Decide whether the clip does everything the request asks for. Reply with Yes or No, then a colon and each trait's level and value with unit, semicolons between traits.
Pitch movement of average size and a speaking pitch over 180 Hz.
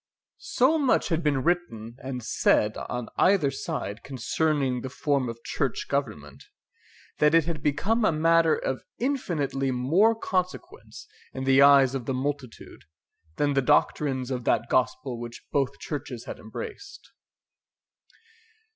No: average, 4.6 semitones; medium, 140 Hz